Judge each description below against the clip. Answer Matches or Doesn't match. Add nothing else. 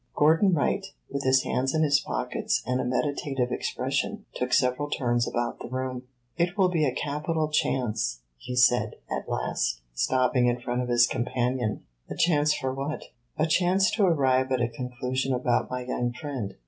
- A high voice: Doesn't match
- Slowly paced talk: Doesn't match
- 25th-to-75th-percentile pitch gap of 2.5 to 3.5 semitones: Matches